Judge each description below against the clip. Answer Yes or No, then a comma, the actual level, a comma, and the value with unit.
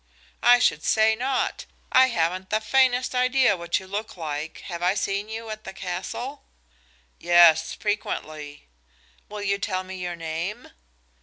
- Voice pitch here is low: No, high, 195 Hz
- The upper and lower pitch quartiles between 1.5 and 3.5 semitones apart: No, average, 4.6 semitones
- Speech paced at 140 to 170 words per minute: Yes, average, 150 wpm